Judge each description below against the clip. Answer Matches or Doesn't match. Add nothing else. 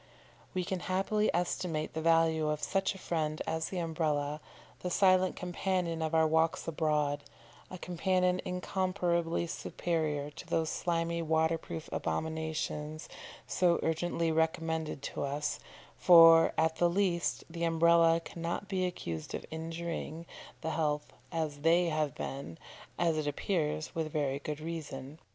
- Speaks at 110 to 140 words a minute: Matches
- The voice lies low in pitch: Doesn't match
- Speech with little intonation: Matches